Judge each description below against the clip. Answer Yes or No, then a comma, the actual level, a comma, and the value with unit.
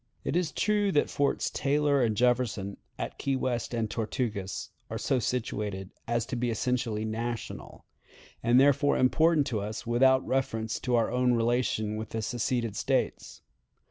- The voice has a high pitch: No, low, 120 Hz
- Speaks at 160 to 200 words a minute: No, average, 150 wpm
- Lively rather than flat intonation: No, average, 3.0 semitones